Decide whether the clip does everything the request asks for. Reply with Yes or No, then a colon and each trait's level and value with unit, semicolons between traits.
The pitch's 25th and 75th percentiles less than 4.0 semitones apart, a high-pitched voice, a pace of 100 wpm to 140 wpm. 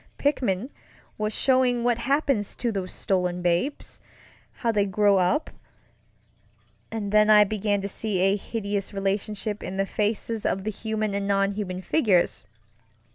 Yes: narrow, 2.4 semitones; high, 205 Hz; slow, 135 wpm